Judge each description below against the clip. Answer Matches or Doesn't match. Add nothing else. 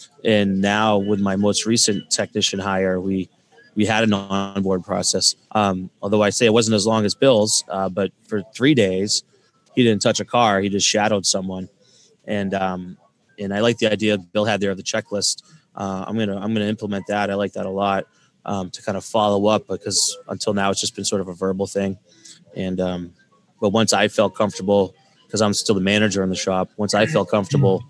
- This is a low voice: Matches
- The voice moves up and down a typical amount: Doesn't match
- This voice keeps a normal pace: Doesn't match